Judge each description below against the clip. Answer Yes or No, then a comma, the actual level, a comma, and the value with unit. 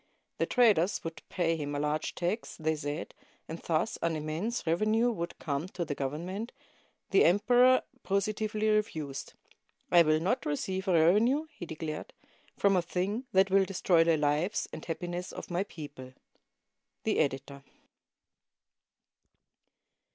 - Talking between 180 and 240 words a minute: No, average, 140 wpm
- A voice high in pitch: No, medium, 175 Hz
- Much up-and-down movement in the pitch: No, average, 4.7 semitones